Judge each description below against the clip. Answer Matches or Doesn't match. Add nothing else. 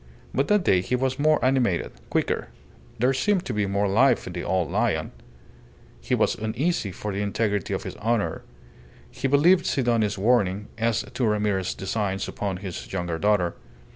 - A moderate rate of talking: Matches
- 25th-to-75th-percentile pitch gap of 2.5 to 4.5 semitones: Doesn't match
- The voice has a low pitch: Matches